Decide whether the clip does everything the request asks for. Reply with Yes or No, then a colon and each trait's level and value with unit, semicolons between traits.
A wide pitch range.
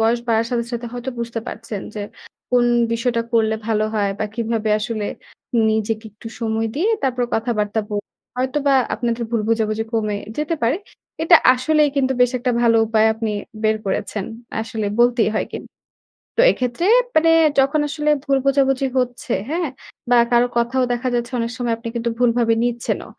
No: narrow, 2.5 semitones